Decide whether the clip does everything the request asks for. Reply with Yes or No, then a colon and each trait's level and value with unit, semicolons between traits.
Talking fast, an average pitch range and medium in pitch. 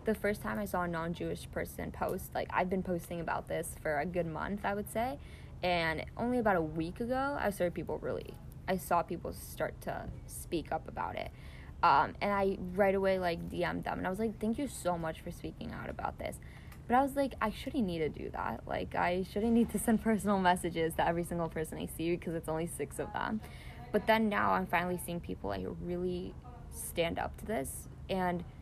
Yes: fast, 225 wpm; average, 3.7 semitones; medium, 180 Hz